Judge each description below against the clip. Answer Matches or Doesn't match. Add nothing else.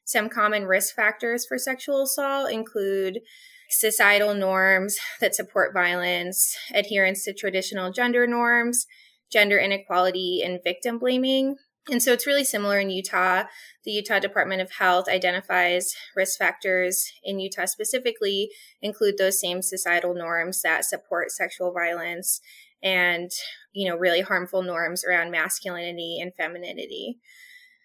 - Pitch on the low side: Doesn't match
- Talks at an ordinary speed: Doesn't match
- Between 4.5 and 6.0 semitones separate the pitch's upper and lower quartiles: Matches